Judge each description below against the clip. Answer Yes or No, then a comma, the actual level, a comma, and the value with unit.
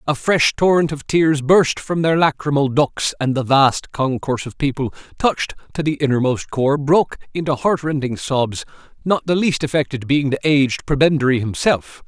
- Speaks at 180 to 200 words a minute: No, average, 170 wpm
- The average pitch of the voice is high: No, medium, 140 Hz